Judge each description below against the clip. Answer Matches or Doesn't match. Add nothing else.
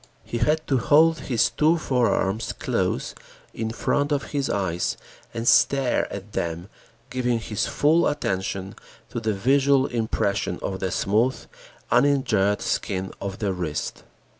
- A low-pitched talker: Matches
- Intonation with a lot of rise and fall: Matches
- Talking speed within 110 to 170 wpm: Matches